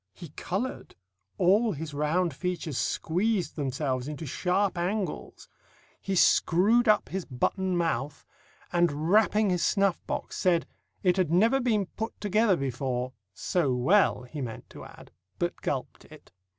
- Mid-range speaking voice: Yes, medium, 180 Hz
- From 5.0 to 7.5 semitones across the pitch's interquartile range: Yes, average, 5.3 semitones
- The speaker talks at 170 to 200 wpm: No, average, 140 wpm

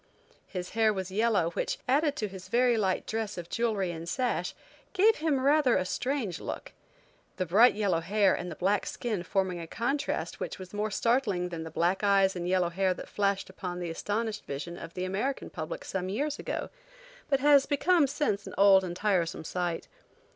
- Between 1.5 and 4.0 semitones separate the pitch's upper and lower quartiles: No, average, 4.9 semitones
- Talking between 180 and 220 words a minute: Yes, average, 190 wpm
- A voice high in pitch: Yes, high, 195 Hz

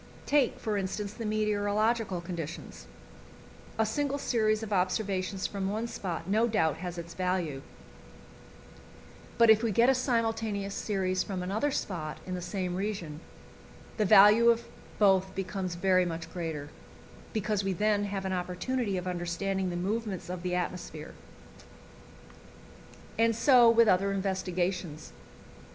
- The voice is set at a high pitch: Yes, high, 195 Hz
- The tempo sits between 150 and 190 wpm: No, slow, 135 wpm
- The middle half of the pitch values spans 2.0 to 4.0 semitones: Yes, average, 3.2 semitones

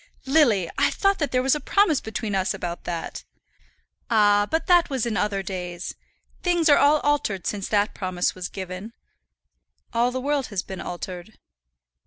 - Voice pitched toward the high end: Yes, high, 210 Hz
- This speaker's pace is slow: No, average, 170 wpm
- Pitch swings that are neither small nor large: No, wide, 7.4 semitones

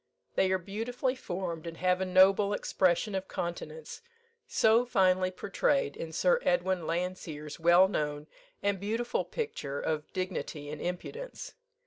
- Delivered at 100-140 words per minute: Yes, slow, 135 wpm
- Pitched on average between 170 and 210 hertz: Yes, medium, 185 Hz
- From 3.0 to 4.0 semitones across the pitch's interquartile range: Yes, average, 3.6 semitones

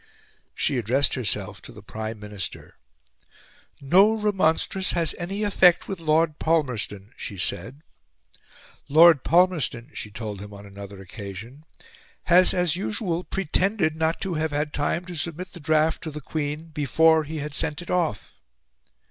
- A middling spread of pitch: No, wide, 6.7 semitones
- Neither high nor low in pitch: Yes, medium, 155 Hz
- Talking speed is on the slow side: No, average, 150 wpm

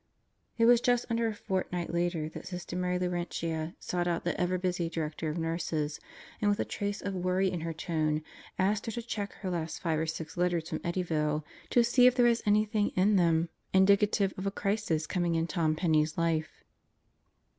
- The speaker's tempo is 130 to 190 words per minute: No, average, 200 wpm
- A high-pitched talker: No, medium, 180 Hz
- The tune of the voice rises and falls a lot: No, average, 3.7 semitones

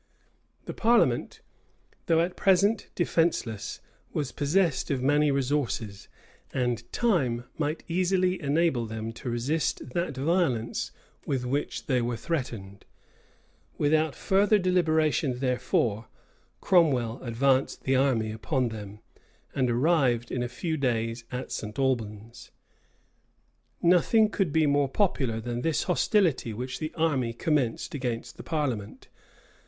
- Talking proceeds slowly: Yes, slow, 120 wpm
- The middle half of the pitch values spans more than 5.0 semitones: Yes, wide, 5.5 semitones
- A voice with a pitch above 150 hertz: No, low, 135 Hz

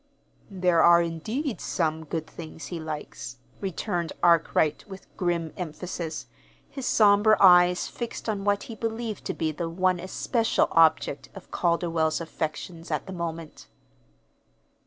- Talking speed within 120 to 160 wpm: Yes, slow, 135 wpm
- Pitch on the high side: No, medium, 175 Hz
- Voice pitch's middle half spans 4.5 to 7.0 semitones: No, average, 3.4 semitones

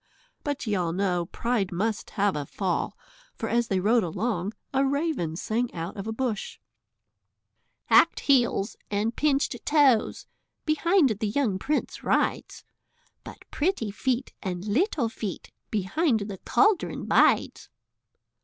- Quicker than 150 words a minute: No, slow, 135 wpm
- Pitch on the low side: No, high, 220 Hz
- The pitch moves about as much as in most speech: No, wide, 5.8 semitones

